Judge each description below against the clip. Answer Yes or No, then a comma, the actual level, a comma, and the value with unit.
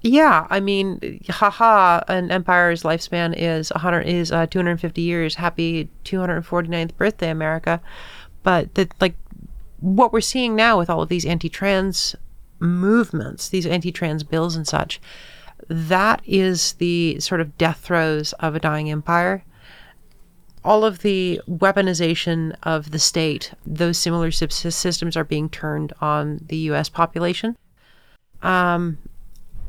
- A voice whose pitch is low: No, medium, 170 Hz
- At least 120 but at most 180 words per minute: Yes, average, 145 wpm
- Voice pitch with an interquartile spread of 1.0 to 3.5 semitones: Yes, narrow, 2.4 semitones